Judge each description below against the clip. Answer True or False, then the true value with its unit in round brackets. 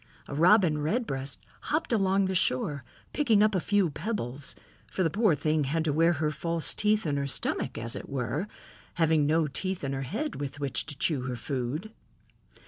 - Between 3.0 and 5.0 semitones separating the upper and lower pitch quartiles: False (5.4 semitones)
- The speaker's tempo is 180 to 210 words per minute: True (190 wpm)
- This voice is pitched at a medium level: True (155 Hz)